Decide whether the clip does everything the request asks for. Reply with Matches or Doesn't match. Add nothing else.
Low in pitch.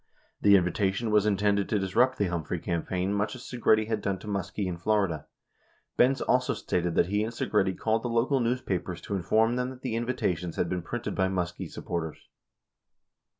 Matches